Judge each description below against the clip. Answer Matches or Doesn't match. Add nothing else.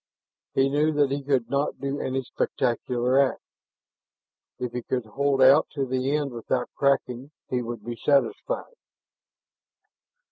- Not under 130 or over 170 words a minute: Matches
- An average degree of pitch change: Doesn't match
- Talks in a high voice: Doesn't match